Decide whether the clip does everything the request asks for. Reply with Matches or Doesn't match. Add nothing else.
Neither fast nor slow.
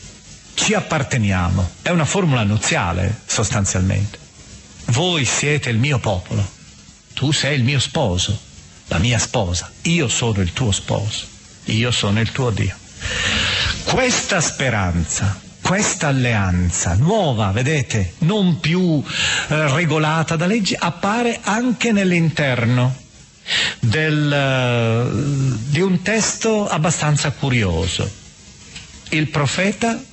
Doesn't match